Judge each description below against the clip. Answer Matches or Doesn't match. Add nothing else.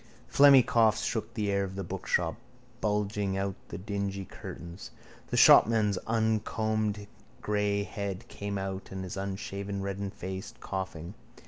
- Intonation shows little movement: Matches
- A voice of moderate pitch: Doesn't match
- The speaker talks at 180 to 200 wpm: Doesn't match